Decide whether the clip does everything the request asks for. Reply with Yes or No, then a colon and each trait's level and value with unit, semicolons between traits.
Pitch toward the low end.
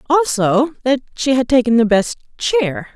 No: very high, 250 Hz